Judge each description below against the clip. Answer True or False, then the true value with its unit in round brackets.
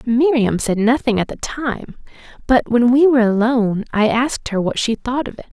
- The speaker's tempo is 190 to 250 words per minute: True (205 wpm)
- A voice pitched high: True (240 Hz)